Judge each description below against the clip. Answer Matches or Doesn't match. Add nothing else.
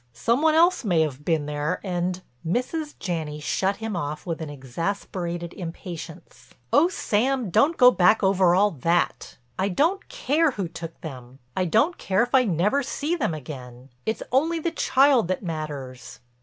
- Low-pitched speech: Doesn't match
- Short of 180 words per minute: Matches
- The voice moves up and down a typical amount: Doesn't match